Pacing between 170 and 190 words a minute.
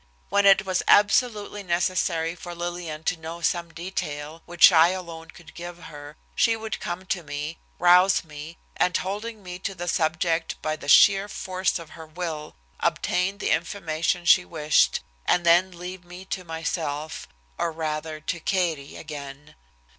No: average, 160 wpm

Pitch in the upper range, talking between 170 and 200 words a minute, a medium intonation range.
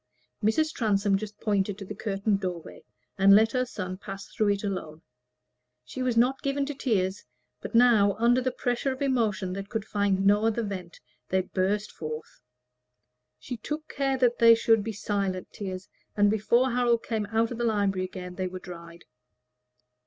Yes: high, 205 Hz; average, 175 wpm; average, 3.6 semitones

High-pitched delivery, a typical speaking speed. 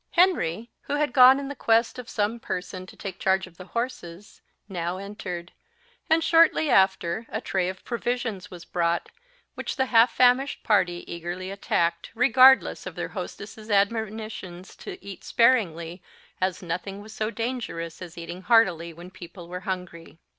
Yes: high, 195 Hz; average, 155 wpm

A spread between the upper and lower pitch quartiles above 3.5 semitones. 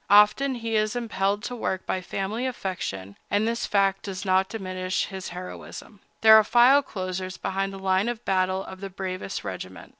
No: average, 2.8 semitones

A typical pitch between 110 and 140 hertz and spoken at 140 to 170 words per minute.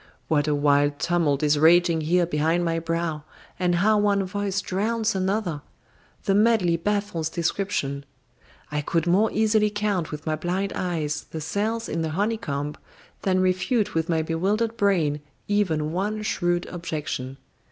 No: medium, 175 Hz; average, 150 wpm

